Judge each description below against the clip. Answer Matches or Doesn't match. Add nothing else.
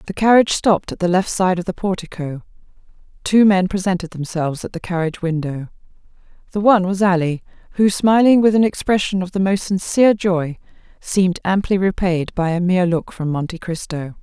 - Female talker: Matches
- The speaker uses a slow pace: Doesn't match